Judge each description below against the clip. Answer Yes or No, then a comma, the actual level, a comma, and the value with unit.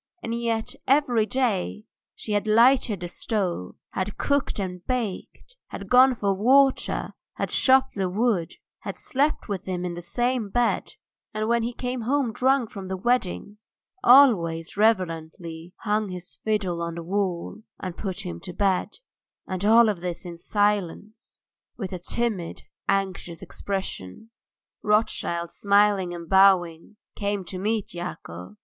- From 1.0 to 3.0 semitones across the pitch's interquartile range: No, average, 4.4 semitones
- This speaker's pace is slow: No, average, 145 wpm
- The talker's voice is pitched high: Yes, high, 200 Hz